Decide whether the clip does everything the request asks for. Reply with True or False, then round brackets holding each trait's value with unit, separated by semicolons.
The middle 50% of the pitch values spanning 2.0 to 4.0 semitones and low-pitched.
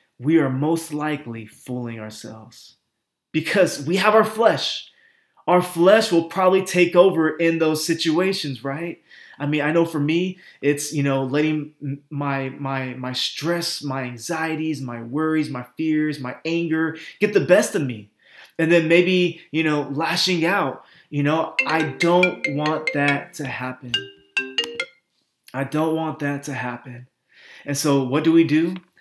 False (3.7 semitones; 155 Hz)